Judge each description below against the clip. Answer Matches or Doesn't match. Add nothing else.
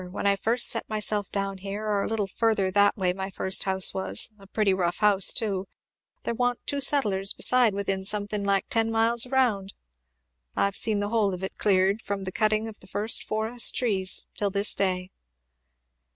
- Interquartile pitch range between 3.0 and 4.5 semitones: Doesn't match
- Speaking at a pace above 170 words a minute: Matches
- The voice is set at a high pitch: Matches